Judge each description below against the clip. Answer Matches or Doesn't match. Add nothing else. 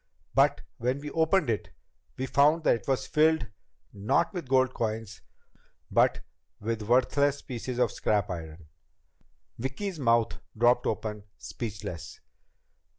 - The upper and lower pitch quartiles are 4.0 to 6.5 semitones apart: Matches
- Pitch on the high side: Doesn't match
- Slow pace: Matches